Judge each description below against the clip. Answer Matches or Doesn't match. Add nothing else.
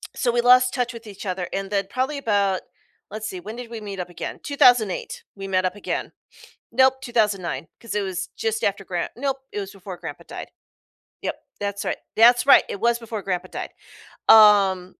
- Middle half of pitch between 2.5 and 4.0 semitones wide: Matches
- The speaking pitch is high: Matches